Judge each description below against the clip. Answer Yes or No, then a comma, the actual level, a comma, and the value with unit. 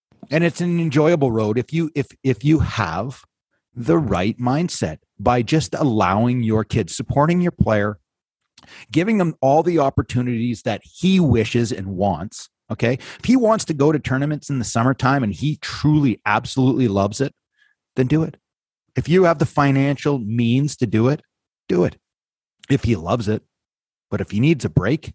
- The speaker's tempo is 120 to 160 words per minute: No, average, 175 wpm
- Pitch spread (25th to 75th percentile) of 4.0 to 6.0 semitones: Yes, wide, 5.4 semitones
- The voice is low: Yes, low, 130 Hz